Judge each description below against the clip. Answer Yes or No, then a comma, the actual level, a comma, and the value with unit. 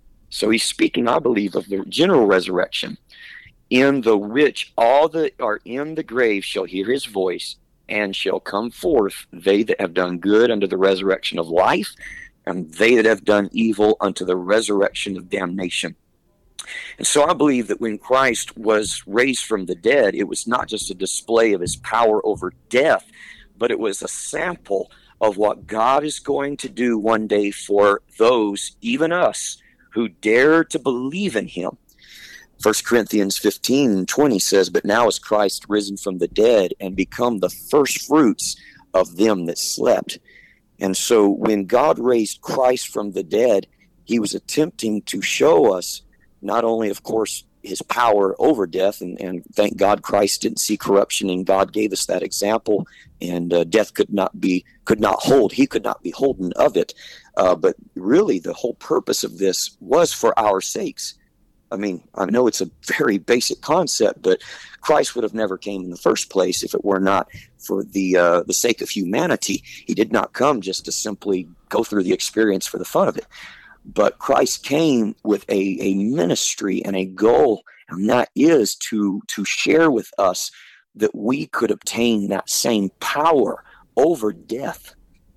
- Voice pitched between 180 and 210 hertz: No, low, 105 Hz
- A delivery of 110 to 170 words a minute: No, average, 180 wpm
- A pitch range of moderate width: Yes, average, 4.1 semitones